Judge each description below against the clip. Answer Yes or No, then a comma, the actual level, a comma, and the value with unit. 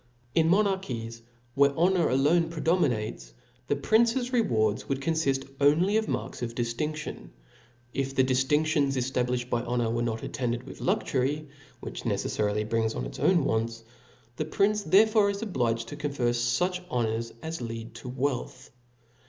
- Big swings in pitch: Yes, wide, 5.8 semitones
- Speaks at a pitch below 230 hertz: Yes, low, 135 Hz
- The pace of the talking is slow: No, average, 150 wpm